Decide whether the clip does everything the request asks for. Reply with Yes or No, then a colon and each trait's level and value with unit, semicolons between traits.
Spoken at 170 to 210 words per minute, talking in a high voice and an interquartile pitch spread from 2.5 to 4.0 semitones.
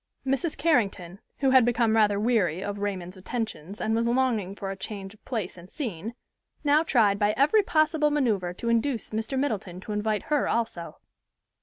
No: average, 175 wpm; high, 220 Hz; average, 4.8 semitones